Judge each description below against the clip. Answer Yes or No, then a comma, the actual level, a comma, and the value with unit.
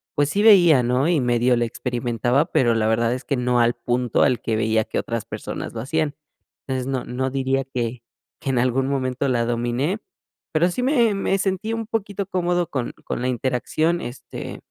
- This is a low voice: Yes, low, 130 Hz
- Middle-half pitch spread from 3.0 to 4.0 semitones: No, average, 5.1 semitones